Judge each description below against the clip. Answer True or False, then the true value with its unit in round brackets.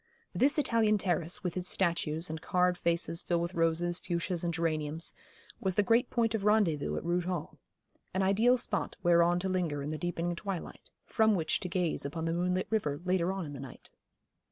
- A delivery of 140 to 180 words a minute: False (195 wpm)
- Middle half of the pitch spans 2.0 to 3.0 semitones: True (2.6 semitones)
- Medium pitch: True (175 Hz)